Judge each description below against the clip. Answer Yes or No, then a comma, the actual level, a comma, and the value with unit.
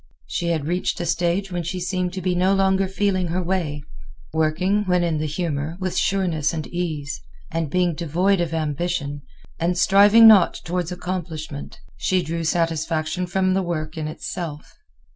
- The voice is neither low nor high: Yes, medium, 175 Hz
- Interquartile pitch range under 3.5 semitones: Yes, average, 2.7 semitones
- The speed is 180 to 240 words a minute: No, average, 165 wpm